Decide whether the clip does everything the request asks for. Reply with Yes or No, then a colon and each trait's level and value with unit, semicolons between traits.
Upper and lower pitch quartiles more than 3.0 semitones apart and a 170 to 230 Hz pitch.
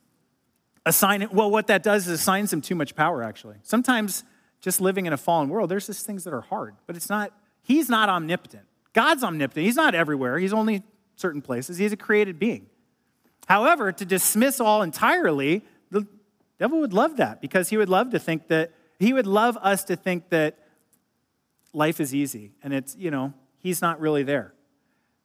Yes: average, 5.3 semitones; high, 190 Hz